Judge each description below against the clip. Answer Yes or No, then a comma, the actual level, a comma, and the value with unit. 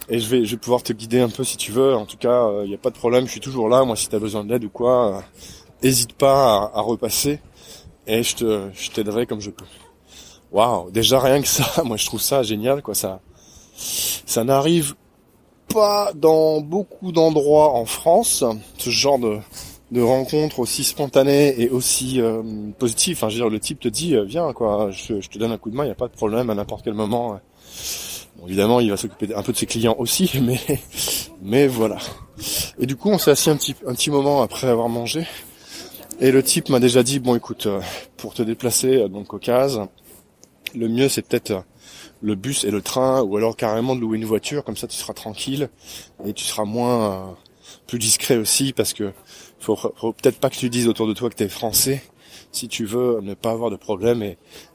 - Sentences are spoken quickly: Yes, fast, 225 wpm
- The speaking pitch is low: Yes, low, 120 Hz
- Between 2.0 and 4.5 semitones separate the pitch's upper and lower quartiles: Yes, average, 3.7 semitones